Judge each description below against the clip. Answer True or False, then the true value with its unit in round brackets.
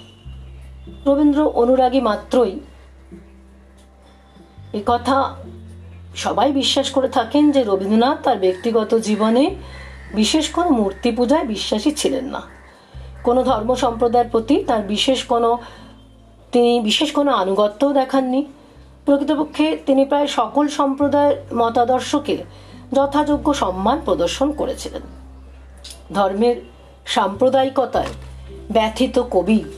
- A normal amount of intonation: False (8.1 semitones)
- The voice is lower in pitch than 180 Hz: False (240 Hz)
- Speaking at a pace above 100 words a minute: False (95 wpm)